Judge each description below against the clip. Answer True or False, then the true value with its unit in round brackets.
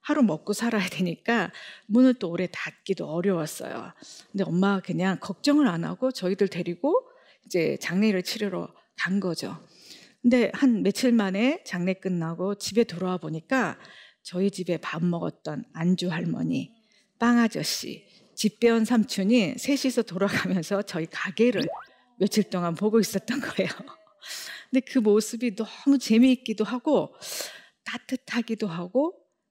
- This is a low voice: False (210 Hz)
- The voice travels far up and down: False (4.7 semitones)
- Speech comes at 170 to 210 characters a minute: False (290 characters per minute)